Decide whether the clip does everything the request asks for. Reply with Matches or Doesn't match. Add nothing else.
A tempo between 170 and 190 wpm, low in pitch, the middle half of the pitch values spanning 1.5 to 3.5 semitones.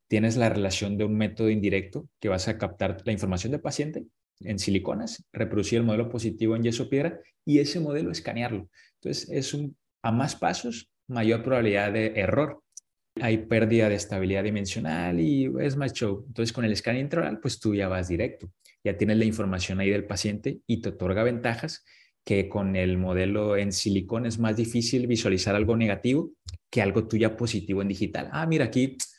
Matches